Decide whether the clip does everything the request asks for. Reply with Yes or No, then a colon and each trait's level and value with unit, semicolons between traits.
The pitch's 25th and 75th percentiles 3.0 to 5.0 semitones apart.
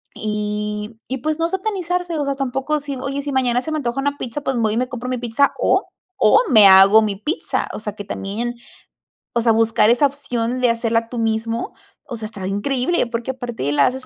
Yes: average, 3.9 semitones